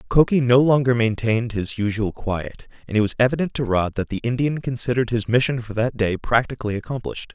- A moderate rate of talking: Yes, average, 195 wpm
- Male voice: Yes, male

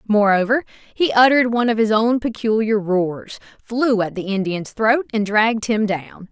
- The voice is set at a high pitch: Yes, high, 220 Hz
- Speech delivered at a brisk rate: No, average, 170 wpm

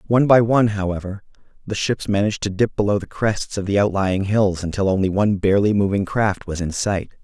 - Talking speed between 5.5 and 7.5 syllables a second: Yes, 6.0 syllables/s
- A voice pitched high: No, low, 100 Hz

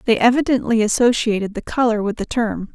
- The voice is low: No, high, 225 Hz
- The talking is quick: No, average, 175 wpm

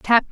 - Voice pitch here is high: Yes, high, 230 Hz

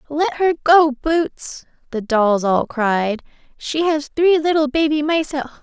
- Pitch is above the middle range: Yes, very high, 285 Hz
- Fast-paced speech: No, average, 170 wpm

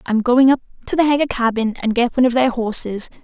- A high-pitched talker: Yes, high, 245 Hz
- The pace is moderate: No, fast, 240 wpm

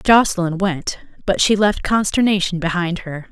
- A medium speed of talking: Yes, average, 145 wpm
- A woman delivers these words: Yes, female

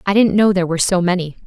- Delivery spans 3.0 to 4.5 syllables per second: No, 7.9 syllables/s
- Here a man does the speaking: No, female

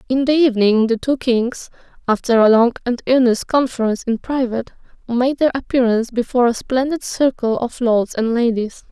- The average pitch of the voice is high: Yes, high, 245 Hz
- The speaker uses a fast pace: No, average, 170 wpm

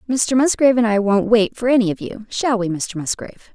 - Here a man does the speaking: No, female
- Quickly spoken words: Yes, fast, 235 wpm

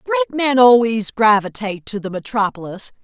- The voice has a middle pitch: No, high, 230 Hz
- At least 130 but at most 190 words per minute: Yes, average, 140 wpm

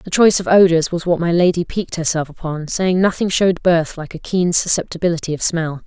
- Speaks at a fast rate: Yes, fast, 215 wpm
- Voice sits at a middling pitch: Yes, medium, 170 Hz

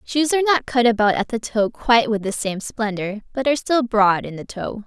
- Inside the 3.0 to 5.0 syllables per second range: No, 5.4 syllables/s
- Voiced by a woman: Yes, female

